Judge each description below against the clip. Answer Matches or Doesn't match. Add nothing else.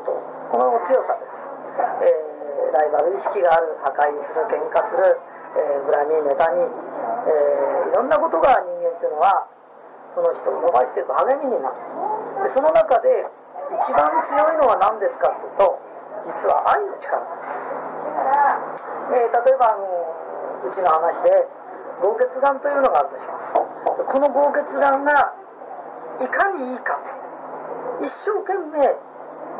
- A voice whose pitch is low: Doesn't match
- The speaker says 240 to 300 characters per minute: Matches